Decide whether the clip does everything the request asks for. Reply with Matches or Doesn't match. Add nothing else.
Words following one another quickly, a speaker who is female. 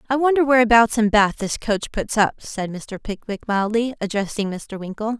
Doesn't match